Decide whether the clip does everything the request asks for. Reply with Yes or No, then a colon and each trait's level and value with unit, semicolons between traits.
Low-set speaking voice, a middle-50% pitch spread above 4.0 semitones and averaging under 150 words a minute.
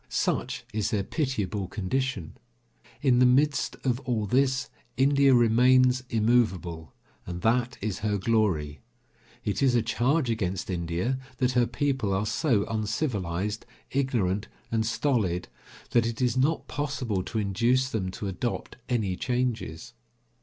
Yes: low, 115 Hz; average, 4.6 semitones; slow, 135 wpm